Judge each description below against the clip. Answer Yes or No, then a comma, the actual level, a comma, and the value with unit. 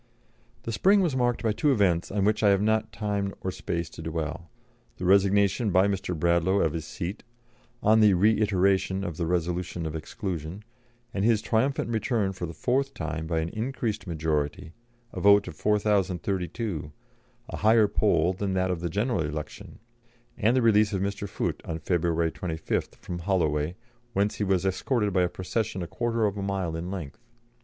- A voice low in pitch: Yes, very low, 95 Hz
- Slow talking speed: No, average, 180 wpm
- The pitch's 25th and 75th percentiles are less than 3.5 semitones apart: No, average, 3.8 semitones